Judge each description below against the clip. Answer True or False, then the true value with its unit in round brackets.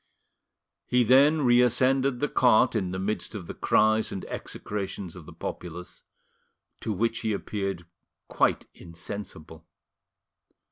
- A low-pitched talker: True (105 Hz)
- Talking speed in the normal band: False (125 wpm)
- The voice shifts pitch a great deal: False (4.8 semitones)